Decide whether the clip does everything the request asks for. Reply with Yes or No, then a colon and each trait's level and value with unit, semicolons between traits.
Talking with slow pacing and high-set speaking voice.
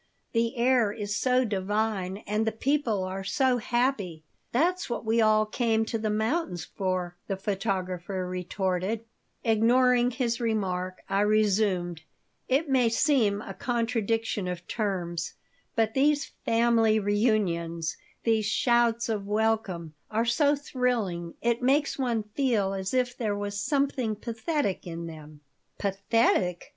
Yes: slow, 130 wpm; high, 220 Hz